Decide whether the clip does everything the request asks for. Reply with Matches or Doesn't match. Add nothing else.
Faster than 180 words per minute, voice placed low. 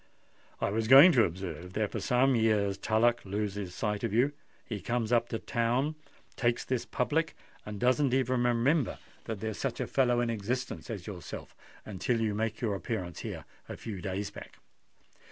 Doesn't match